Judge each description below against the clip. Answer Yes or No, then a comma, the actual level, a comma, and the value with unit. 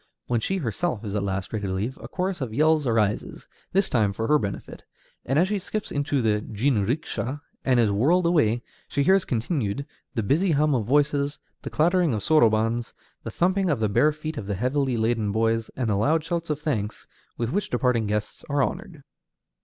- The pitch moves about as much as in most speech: No, wide, 6.0 semitones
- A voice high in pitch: No, low, 130 Hz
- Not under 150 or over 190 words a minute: No, average, 200 wpm